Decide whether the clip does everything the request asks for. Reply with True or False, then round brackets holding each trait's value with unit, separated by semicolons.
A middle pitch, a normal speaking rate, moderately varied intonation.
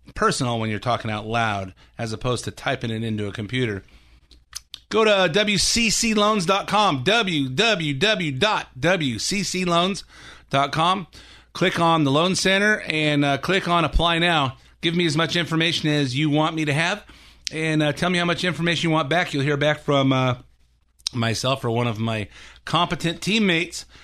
False (155 Hz; 155 wpm; 6.0 semitones)